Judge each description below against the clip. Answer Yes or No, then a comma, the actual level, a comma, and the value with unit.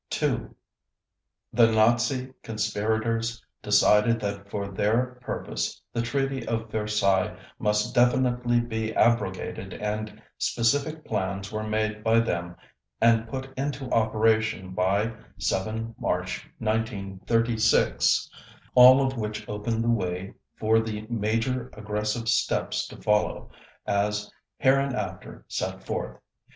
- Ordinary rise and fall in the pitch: No, narrow, 2.1 semitones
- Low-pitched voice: Yes, low, 110 Hz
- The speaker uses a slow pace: Yes, slow, 110 wpm